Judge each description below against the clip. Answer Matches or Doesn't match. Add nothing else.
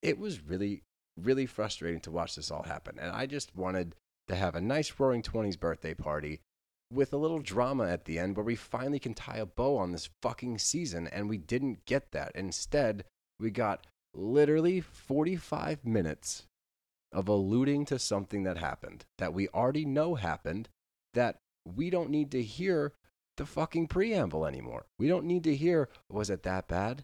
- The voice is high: Doesn't match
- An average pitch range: Doesn't match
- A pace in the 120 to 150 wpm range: Doesn't match